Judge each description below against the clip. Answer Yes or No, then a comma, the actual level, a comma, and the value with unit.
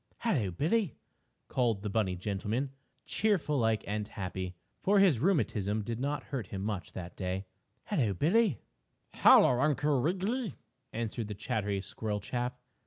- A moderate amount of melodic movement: No, wide, 6.8 semitones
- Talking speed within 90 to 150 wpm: Yes, average, 140 wpm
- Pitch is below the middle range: Yes, low, 115 Hz